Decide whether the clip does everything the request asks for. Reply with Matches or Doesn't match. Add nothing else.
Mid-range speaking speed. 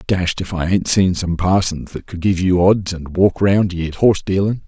Doesn't match